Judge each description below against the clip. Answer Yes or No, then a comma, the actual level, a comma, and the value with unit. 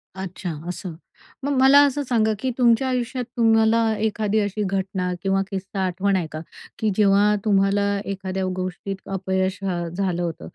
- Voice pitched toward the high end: Yes, high, 195 Hz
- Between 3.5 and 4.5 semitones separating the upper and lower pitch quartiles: No, average, 2.8 semitones